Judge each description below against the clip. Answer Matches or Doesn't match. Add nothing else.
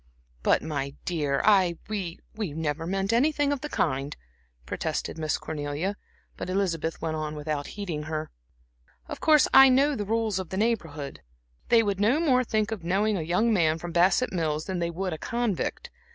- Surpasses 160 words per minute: Matches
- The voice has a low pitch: Doesn't match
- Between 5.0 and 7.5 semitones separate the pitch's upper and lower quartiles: Matches